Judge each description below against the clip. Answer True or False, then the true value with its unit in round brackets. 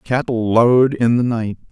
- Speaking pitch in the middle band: False (115 Hz)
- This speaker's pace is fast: False (175 wpm)